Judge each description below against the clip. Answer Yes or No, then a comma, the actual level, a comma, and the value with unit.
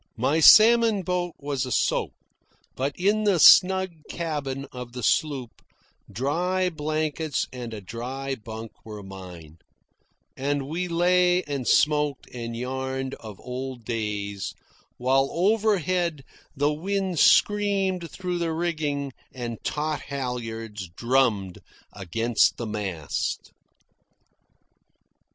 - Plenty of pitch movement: Yes, wide, 6.7 semitones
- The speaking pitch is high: No, low, 135 Hz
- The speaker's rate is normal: No, slow, 110 wpm